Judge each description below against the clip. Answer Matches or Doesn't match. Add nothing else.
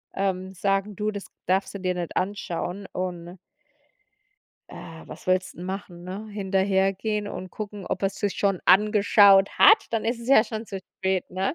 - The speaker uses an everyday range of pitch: Doesn't match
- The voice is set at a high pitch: Matches